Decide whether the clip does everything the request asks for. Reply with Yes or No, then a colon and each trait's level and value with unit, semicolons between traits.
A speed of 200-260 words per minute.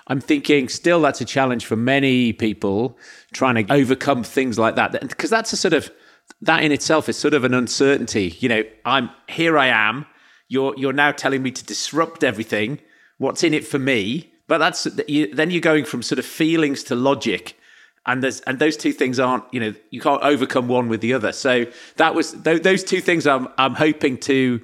Yes: fast, 205 wpm